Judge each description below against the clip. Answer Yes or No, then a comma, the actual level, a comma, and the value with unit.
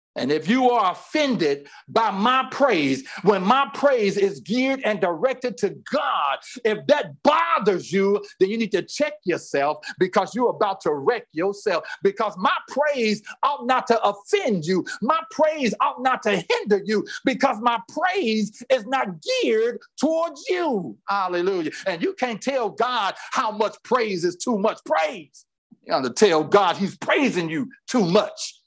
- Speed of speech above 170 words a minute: No, average, 165 wpm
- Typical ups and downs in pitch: No, wide, 6.1 semitones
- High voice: Yes, high, 240 Hz